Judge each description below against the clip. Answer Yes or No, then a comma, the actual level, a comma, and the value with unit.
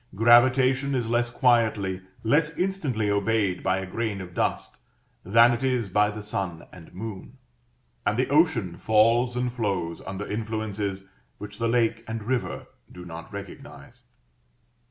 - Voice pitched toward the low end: Yes, low, 110 Hz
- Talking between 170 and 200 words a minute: No, average, 145 wpm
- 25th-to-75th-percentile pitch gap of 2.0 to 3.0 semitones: No, average, 3.6 semitones